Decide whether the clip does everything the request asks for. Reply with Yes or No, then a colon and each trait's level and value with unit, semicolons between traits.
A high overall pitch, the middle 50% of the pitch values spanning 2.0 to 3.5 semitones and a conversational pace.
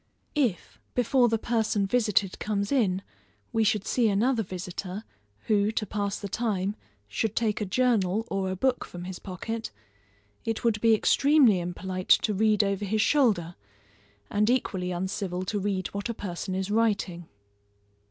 Yes: high, 205 Hz; average, 3.2 semitones; average, 155 wpm